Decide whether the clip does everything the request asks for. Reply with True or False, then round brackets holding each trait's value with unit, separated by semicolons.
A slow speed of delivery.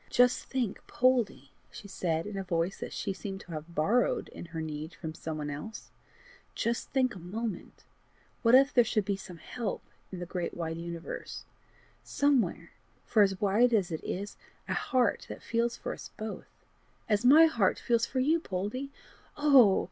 False (180 wpm)